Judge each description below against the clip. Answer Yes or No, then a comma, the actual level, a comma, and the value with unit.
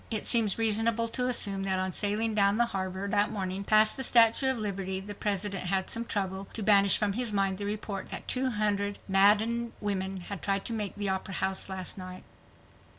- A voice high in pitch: Yes, high, 205 Hz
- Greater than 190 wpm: Yes, fast, 205 wpm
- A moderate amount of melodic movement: No, narrow, 2.3 semitones